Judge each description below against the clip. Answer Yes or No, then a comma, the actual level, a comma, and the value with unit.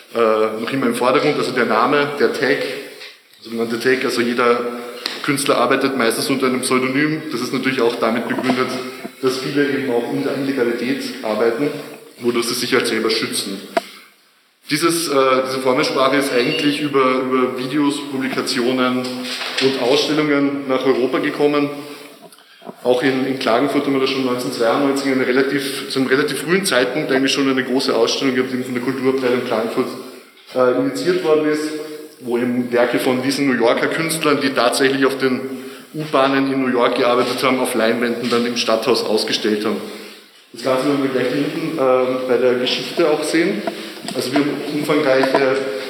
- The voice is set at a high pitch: No, low, 130 Hz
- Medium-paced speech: Yes, average, 165 wpm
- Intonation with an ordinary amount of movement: No, narrow, 2.0 semitones